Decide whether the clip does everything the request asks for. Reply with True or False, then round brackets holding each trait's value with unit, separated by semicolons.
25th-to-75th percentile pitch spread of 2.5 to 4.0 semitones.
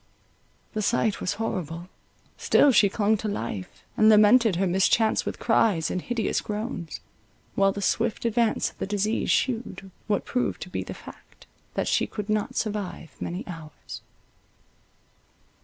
True (3.0 semitones)